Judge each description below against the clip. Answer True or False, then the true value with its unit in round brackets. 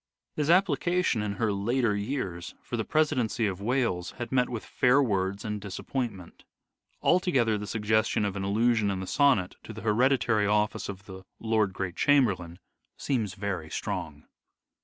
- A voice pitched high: False (110 Hz)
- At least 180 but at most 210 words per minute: False (160 wpm)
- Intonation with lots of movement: False (4.2 semitones)